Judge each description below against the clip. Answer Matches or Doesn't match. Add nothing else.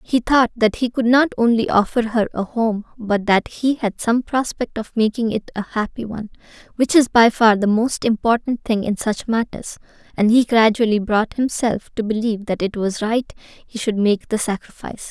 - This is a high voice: Matches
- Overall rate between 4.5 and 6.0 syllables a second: Matches